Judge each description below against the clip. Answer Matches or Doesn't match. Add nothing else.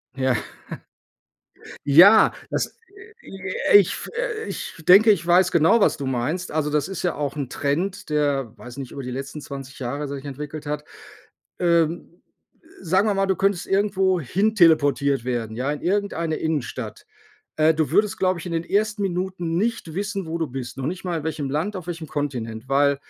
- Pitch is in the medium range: Matches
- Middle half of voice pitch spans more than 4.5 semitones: Matches